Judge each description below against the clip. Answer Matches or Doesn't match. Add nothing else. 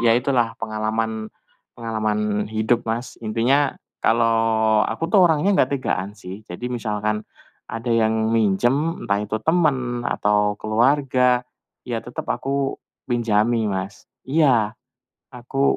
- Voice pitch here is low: Matches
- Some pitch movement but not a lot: Matches